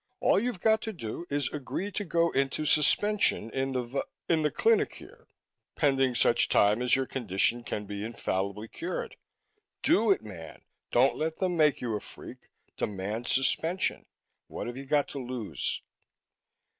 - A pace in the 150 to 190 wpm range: Yes, average, 165 wpm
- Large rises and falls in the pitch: Yes, wide, 6.5 semitones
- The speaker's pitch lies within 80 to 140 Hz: Yes, low, 135 Hz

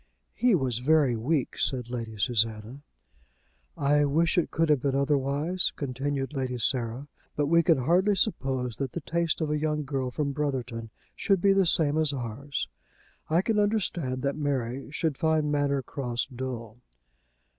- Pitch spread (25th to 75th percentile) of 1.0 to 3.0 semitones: No, average, 3.8 semitones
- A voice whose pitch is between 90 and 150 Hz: Yes, medium, 140 Hz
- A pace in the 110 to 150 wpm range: No, average, 160 wpm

